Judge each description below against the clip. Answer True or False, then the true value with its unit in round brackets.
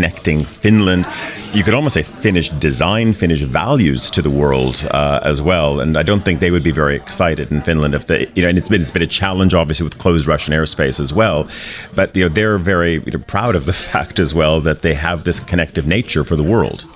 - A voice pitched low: True (85 Hz)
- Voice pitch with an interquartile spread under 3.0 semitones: False (3.9 semitones)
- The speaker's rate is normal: False (235 wpm)